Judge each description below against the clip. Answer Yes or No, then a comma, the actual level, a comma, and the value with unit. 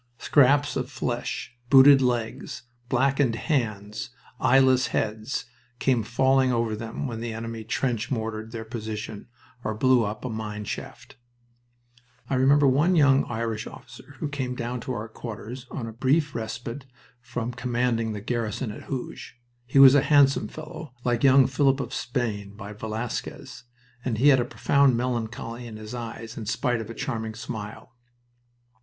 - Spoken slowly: No, average, 160 wpm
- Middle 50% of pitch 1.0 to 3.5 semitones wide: Yes, average, 3.1 semitones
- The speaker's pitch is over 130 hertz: No, low, 120 Hz